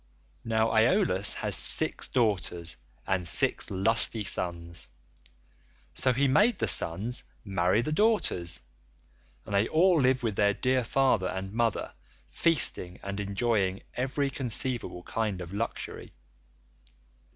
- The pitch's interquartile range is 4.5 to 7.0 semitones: Yes, wide, 5.4 semitones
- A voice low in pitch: Yes, low, 110 Hz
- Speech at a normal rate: No, slow, 120 wpm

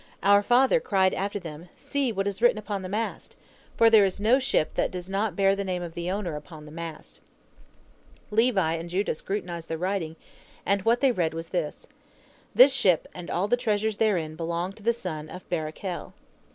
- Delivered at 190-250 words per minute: Yes, average, 195 wpm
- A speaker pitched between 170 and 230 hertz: Yes, high, 190 Hz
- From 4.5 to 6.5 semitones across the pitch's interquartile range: No, average, 4.1 semitones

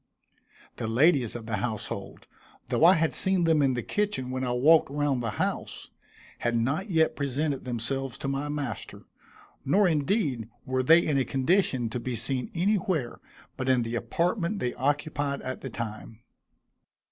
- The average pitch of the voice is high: No, low, 135 Hz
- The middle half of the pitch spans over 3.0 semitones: Yes, average, 4.7 semitones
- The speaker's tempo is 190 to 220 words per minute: No, average, 165 wpm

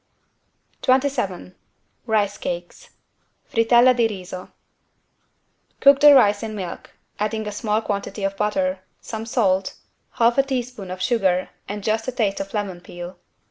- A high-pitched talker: Yes, high, 210 Hz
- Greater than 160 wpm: No, average, 140 wpm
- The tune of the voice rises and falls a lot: No, average, 3.7 semitones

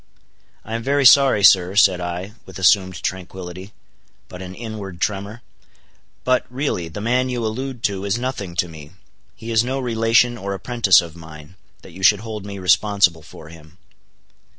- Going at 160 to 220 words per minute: Yes, average, 165 wpm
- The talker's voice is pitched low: Yes, low, 100 Hz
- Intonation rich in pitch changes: No, average, 4.2 semitones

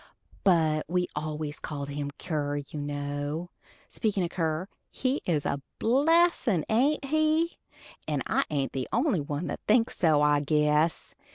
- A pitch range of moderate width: No, wide, 7.4 semitones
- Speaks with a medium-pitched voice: Yes, medium, 155 Hz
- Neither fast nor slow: Yes, average, 150 wpm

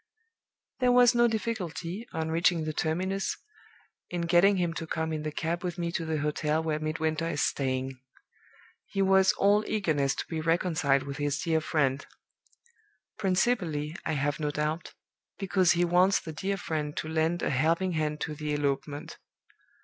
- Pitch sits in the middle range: Yes, medium, 160 Hz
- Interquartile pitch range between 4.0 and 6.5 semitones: No, average, 3.3 semitones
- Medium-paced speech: Yes, average, 165 wpm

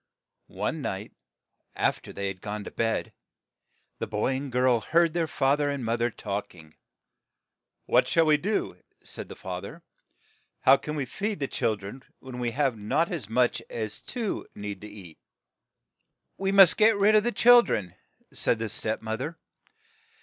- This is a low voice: Yes, low, 125 Hz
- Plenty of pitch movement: Yes, wide, 7.6 semitones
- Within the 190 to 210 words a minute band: Yes, average, 195 wpm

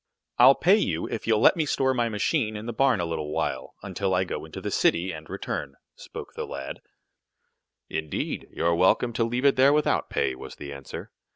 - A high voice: No, low, 105 Hz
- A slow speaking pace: No, fast, 205 wpm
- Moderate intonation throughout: No, wide, 7.5 semitones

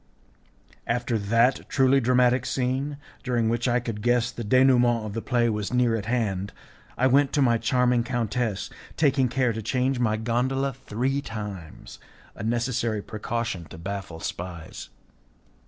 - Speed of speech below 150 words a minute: No, average, 155 wpm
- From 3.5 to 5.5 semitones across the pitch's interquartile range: No, average, 2.8 semitones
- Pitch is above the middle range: No, low, 120 Hz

